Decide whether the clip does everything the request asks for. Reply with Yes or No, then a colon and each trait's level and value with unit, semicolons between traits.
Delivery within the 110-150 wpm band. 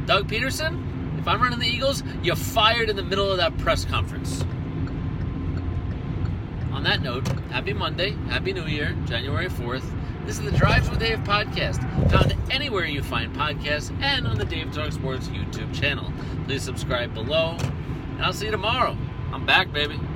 No: average, 170 wpm